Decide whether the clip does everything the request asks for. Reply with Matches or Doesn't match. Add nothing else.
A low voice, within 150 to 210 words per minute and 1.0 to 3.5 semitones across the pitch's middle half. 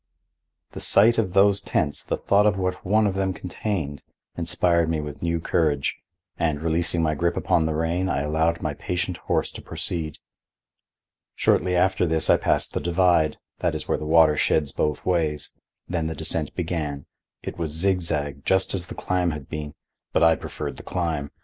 Matches